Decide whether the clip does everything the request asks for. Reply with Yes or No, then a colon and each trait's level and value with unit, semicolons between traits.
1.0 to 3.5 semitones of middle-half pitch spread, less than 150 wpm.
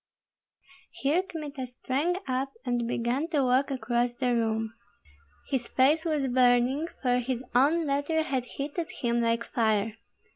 Yes: average, 3.0 semitones; average, 140 wpm